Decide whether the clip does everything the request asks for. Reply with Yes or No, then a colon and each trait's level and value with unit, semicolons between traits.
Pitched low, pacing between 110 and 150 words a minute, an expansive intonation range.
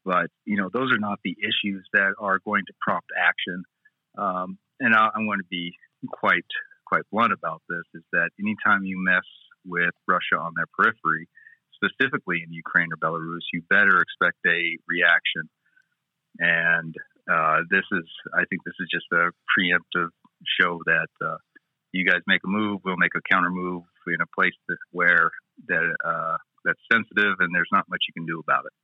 No: very low, 95 Hz; average, 180 wpm; wide, 8.7 semitones